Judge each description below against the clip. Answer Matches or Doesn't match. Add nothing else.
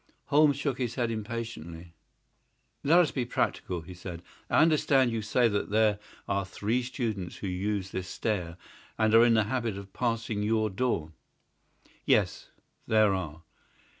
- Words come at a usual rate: Matches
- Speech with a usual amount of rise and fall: Matches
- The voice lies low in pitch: Matches